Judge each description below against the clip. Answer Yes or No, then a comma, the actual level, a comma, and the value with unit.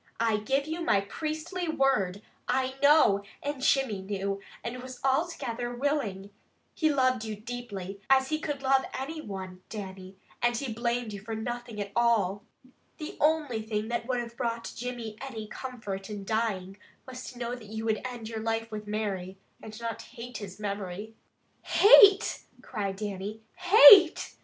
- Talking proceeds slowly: No, average, 160 wpm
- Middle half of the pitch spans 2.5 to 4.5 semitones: Yes, average, 4.2 semitones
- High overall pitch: Yes, high, 230 Hz